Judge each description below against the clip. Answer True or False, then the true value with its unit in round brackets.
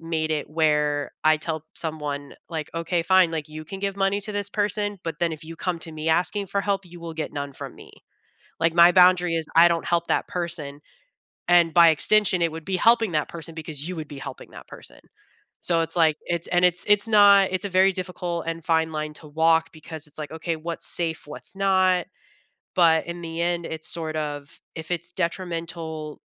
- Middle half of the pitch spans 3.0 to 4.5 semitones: False (2.4 semitones)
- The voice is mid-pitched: True (165 Hz)